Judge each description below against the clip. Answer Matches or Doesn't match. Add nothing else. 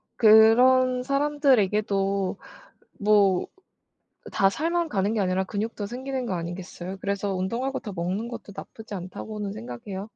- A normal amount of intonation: Matches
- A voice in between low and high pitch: Doesn't match